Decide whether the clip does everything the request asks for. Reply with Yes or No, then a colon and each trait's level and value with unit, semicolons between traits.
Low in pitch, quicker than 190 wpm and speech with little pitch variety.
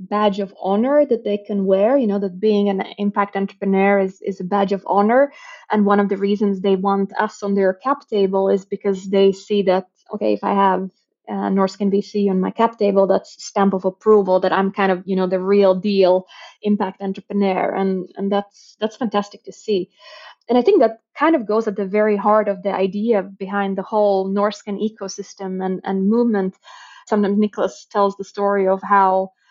No: high, 200 Hz; average, 200 wpm; narrow, 1.4 semitones